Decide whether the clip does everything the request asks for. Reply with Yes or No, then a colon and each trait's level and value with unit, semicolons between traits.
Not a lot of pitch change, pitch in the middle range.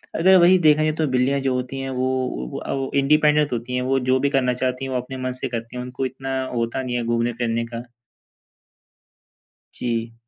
No: narrow, 1.8 semitones; low, 130 Hz